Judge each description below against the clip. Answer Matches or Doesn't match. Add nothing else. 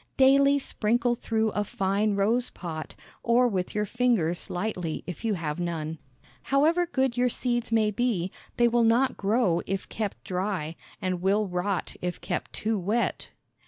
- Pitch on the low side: Doesn't match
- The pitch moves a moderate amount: Matches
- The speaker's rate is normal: Matches